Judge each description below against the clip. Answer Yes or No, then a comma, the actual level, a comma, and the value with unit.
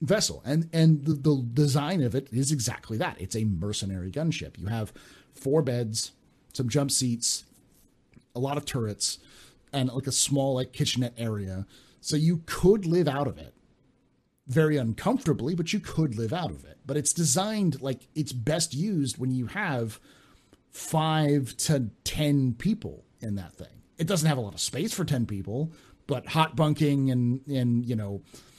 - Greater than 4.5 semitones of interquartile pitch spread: Yes, average, 5.0 semitones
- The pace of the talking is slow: No, average, 175 wpm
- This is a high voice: No, low, 135 Hz